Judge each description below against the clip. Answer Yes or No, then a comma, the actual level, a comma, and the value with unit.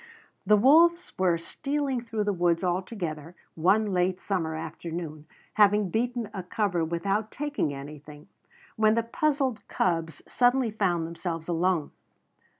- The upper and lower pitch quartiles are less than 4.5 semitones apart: No, average, 5.2 semitones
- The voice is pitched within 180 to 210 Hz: Yes, high, 190 Hz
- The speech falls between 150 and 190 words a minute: No, slow, 135 wpm